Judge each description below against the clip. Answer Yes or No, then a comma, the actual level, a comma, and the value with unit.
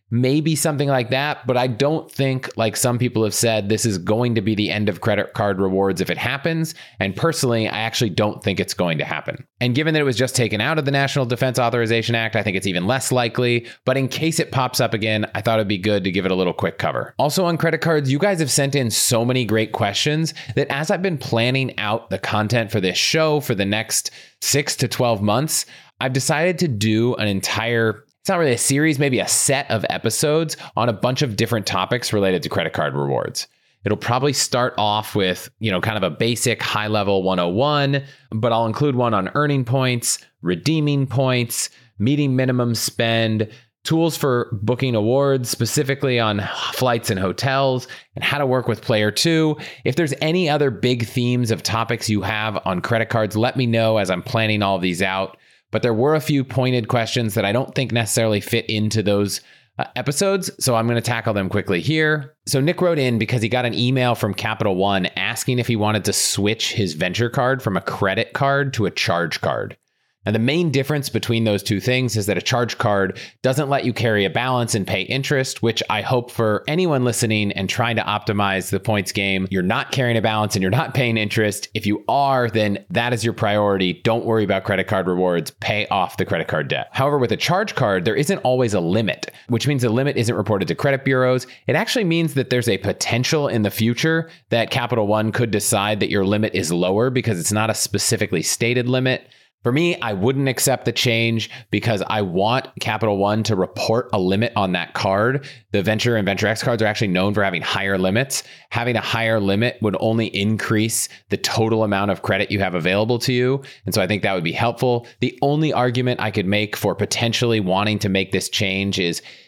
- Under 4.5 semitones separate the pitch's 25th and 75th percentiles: Yes, average, 3.8 semitones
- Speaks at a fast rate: Yes, fast, 220 wpm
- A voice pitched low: Yes, low, 115 Hz